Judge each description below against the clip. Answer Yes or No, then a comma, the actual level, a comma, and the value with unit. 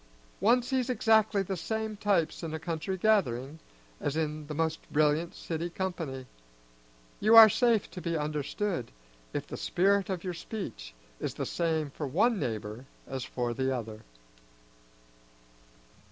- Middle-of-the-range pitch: Yes, medium, 165 Hz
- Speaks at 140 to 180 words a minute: Yes, average, 145 wpm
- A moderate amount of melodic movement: No, wide, 5.9 semitones